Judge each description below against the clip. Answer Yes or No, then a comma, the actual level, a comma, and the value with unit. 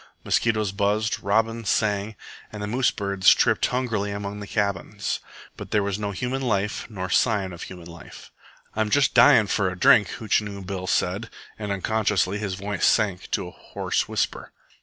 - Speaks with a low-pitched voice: Yes, low, 105 Hz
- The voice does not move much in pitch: Yes, narrow, 2.0 semitones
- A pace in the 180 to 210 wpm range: No, average, 165 wpm